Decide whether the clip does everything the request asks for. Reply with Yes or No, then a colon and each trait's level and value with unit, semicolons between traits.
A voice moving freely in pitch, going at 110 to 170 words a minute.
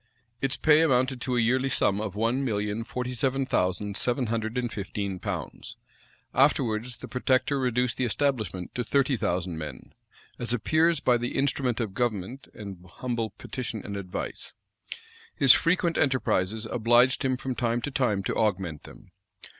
No: average, 3.9 semitones; average, 160 wpm